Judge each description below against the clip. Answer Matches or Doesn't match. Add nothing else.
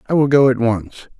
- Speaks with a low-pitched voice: Matches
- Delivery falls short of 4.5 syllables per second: Doesn't match